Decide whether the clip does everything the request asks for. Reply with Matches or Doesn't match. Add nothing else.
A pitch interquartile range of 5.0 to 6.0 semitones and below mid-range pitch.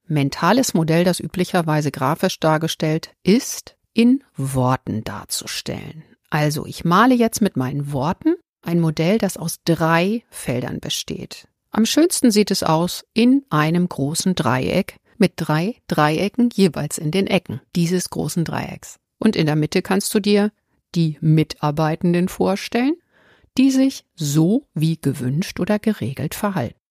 Doesn't match